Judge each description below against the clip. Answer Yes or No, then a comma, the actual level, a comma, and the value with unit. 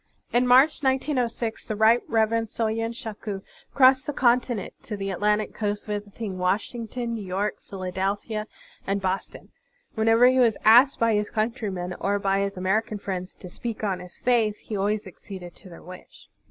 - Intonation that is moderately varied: Yes, average, 3.0 semitones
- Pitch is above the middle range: Yes, high, 215 Hz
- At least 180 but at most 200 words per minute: No, average, 165 wpm